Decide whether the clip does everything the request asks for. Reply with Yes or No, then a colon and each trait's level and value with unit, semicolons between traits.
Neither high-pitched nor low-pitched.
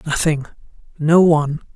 Yes: medium, 155 Hz